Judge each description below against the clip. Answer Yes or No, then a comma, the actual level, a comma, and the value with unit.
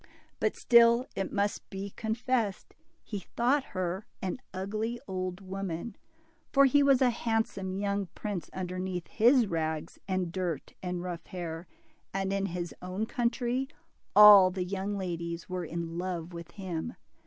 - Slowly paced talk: No, average, 155 wpm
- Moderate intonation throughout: Yes, average, 3.7 semitones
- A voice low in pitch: No, high, 190 Hz